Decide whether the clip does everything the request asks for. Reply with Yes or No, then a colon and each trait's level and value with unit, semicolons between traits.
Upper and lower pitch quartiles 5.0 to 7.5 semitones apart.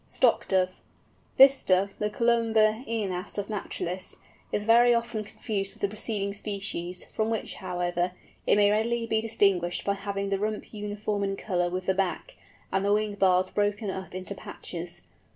No: narrow, 2.5 semitones